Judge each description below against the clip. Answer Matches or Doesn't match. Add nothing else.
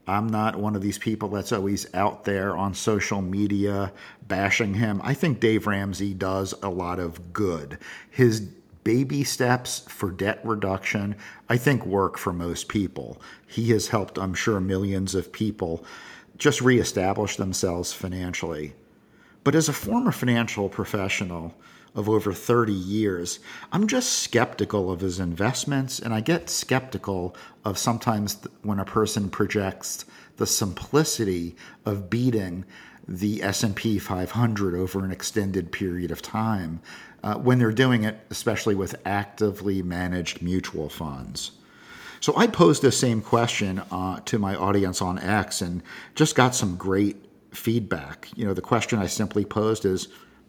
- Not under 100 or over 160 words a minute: Matches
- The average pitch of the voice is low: Matches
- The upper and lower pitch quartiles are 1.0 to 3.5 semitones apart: Matches